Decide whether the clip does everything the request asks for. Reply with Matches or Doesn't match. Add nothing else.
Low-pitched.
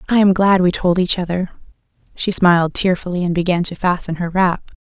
Doesn't match